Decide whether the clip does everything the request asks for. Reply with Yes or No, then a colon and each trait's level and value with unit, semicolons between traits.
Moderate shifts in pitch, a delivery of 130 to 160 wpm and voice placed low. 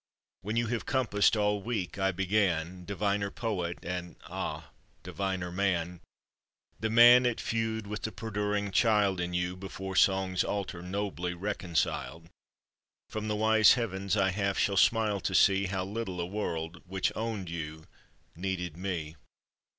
Yes: average, 3.0 semitones; average, 145 wpm; very low, 95 Hz